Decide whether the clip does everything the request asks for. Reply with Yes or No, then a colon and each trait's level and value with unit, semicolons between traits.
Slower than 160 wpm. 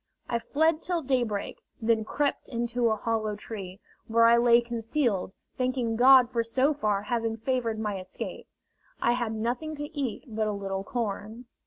No: average, 165 wpm